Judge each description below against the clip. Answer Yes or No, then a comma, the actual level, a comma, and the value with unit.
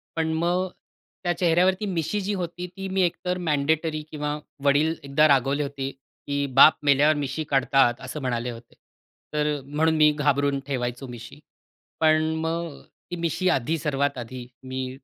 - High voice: No, medium, 150 Hz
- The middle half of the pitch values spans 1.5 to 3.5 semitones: Yes, average, 3.1 semitones